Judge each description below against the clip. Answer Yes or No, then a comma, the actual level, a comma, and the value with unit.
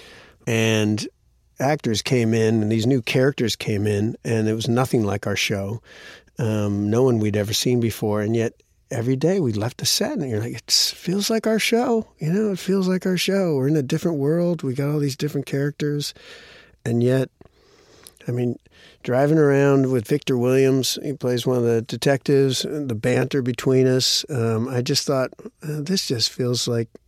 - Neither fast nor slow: Yes, average, 190 wpm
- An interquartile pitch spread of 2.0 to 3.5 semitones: No, average, 4.4 semitones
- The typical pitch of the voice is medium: No, low, 130 Hz